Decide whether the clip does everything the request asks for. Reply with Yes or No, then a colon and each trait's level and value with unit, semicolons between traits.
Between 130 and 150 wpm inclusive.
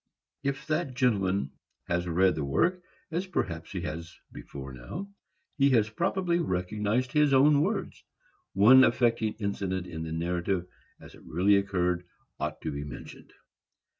Yes: slow, 135 wpm